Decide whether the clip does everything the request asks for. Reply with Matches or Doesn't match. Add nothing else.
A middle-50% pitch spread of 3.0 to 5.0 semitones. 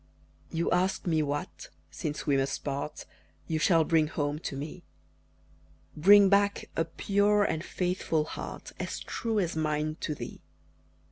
Matches